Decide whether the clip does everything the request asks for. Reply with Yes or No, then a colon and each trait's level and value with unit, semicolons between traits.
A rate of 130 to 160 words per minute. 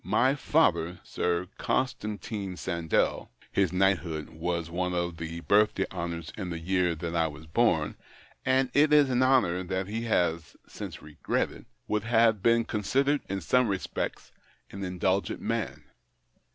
Yes: average, 150 wpm